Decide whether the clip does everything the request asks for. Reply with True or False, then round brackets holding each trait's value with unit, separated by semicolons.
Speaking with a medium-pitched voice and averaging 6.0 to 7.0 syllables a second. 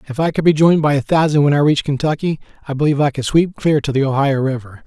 True (145 Hz; 6.8 syllables/s)